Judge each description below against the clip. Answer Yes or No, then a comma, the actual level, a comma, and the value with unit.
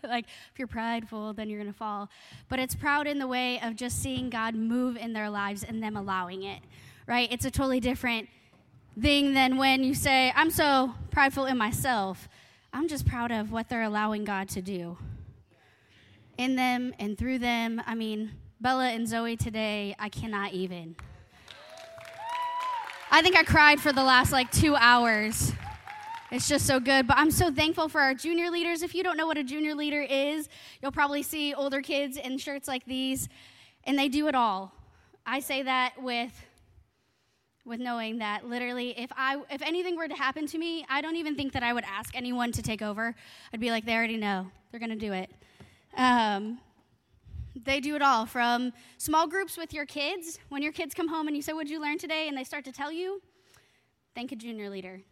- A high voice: Yes, very high, 255 Hz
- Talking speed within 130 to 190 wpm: No, average, 200 wpm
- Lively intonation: No, average, 4.6 semitones